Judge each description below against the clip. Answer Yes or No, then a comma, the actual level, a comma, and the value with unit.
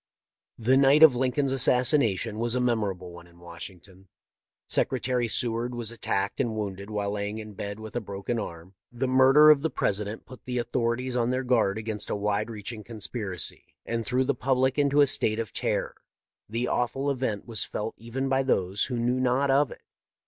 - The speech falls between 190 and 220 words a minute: Yes, average, 195 wpm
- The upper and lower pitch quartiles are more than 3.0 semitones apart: Yes, average, 3.7 semitones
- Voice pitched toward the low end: Yes, low, 115 Hz